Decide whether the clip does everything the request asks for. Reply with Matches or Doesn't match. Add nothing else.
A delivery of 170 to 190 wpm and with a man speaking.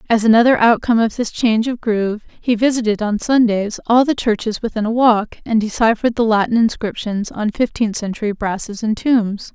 Doesn't match